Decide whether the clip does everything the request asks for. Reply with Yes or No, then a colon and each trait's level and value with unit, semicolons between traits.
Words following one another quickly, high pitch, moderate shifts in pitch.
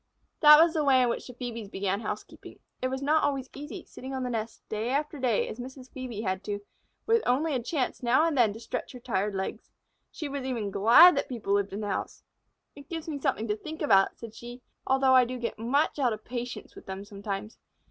Yes: fast, 230 wpm; very high, 250 Hz; average, 4.6 semitones